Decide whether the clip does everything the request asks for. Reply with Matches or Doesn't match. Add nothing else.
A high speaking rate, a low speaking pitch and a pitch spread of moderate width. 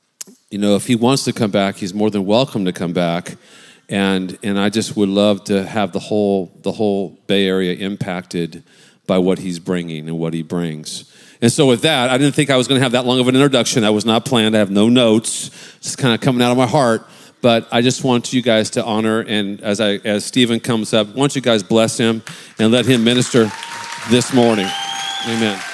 Matches